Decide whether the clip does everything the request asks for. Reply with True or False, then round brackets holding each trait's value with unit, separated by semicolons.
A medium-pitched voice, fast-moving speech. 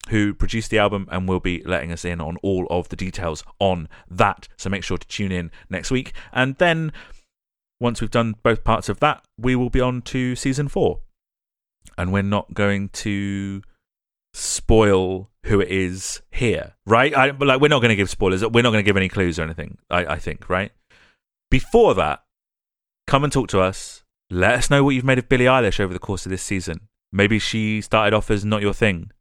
False (105 Hz; 210 wpm)